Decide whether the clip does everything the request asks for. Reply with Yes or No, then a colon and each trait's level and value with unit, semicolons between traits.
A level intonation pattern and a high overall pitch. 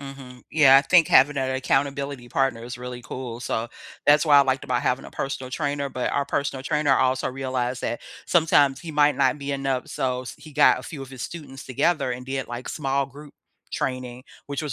No: narrow, 2.0 semitones; low, 135 Hz